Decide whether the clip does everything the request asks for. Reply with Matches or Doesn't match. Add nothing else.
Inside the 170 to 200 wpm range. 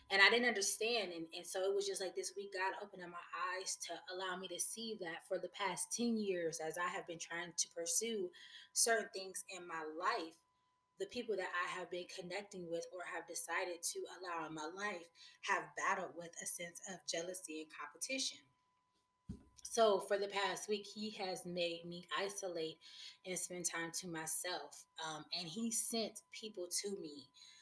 Matches